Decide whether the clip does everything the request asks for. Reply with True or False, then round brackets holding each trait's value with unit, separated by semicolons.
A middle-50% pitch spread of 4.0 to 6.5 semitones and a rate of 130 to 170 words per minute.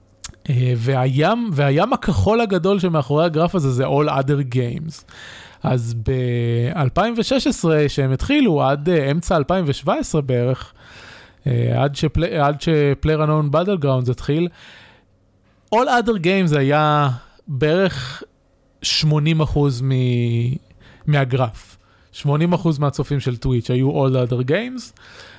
False (4.7 semitones; 100 wpm)